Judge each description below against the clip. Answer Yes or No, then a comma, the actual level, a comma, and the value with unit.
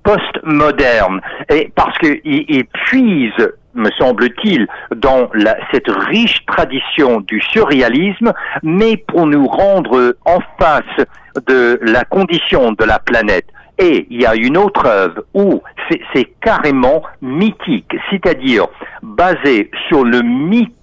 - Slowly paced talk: Yes, slow, 125 wpm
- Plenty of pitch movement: Yes, wide, 8.5 semitones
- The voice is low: No, high, 190 Hz